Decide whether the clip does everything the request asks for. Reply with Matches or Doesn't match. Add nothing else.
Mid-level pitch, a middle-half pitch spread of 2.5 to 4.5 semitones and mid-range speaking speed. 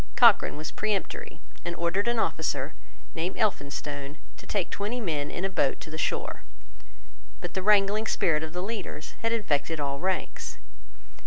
Doesn't match